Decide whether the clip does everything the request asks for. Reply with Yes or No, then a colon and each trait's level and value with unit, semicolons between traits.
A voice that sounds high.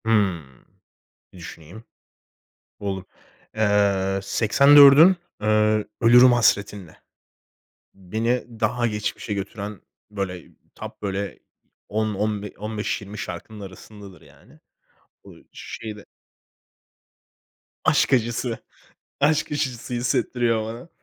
No: low, 105 Hz